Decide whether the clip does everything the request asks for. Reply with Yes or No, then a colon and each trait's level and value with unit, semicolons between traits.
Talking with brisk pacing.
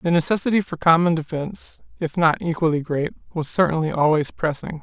No: average, 160 wpm